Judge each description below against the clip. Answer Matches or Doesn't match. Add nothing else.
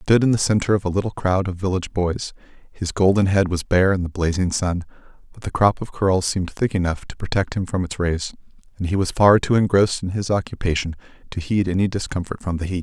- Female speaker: Doesn't match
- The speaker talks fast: Matches